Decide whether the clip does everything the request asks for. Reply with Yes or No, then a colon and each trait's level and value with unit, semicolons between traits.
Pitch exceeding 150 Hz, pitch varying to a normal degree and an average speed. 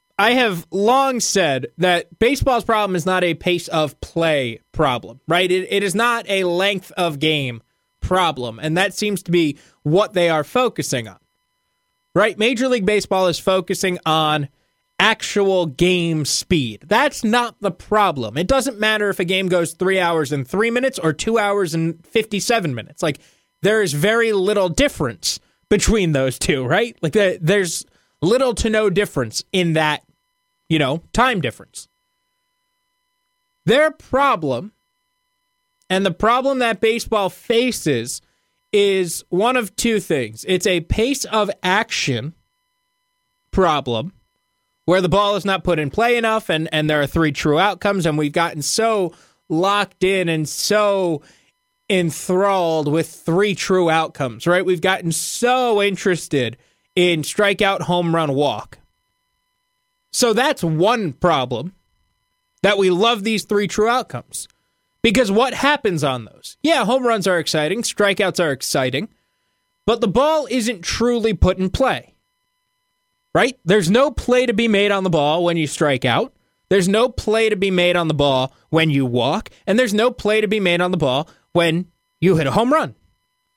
No: high, 190 Hz; wide, 6.1 semitones; average, 160 wpm